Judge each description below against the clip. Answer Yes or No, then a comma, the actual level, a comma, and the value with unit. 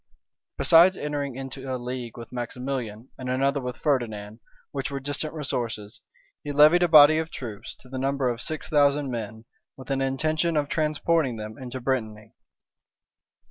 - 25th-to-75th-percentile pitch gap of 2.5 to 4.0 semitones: Yes, average, 3.4 semitones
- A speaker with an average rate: Yes, average, 160 wpm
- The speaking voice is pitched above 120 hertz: Yes, low, 135 Hz